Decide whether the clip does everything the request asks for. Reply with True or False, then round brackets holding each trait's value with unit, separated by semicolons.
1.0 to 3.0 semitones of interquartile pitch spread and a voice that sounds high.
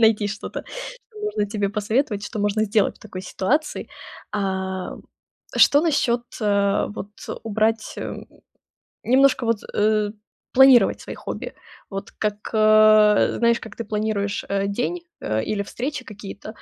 True (2.6 semitones; 215 Hz)